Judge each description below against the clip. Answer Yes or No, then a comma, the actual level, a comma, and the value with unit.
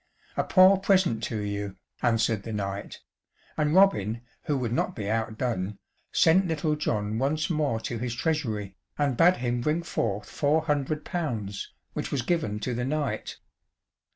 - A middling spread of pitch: No, wide, 6.2 semitones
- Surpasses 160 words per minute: No, average, 155 wpm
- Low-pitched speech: Yes, low, 125 Hz